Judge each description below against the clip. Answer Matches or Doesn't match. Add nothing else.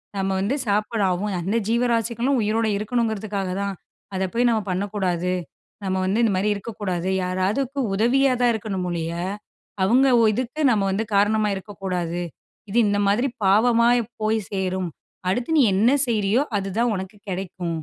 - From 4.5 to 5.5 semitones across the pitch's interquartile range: Doesn't match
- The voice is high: Matches